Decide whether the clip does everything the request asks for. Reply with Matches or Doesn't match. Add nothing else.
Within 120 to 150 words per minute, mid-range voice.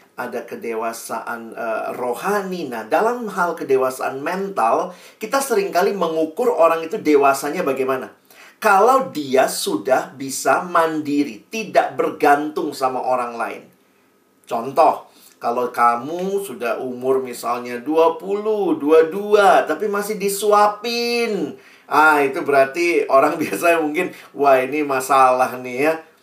Doesn't match